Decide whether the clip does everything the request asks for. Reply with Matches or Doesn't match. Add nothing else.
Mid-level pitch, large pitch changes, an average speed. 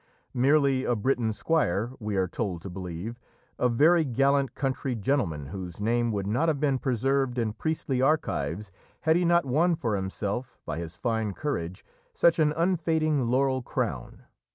Doesn't match